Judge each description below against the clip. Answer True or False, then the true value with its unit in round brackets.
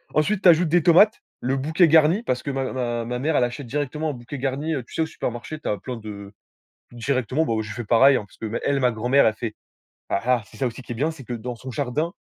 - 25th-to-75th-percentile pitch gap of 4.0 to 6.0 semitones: True (4.3 semitones)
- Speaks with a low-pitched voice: True (130 Hz)